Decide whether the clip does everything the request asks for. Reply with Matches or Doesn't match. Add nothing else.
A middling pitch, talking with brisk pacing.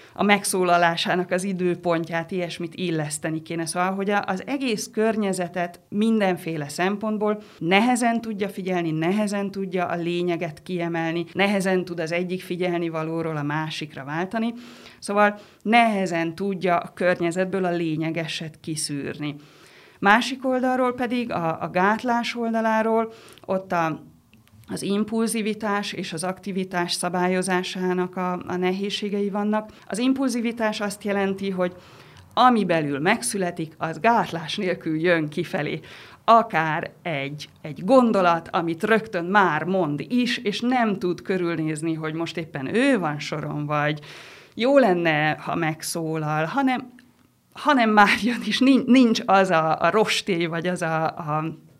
Doesn't match